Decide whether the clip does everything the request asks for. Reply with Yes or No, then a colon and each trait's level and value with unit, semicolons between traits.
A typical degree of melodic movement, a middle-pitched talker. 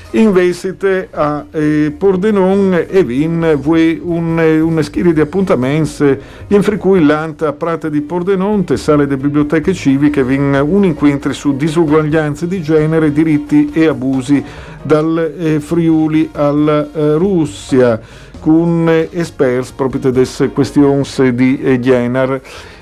Yes: average, 3.0 semitones; medium, 155 Hz